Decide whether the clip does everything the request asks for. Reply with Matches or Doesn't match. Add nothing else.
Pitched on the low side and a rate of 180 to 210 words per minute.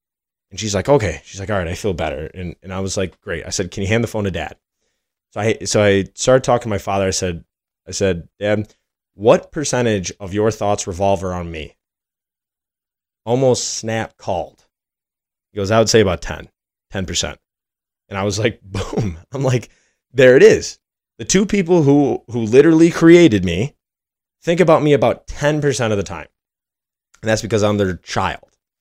Matches